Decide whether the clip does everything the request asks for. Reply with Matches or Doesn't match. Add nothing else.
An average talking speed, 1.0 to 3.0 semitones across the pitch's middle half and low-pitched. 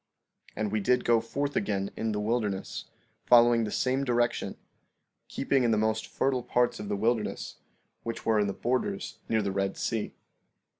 Matches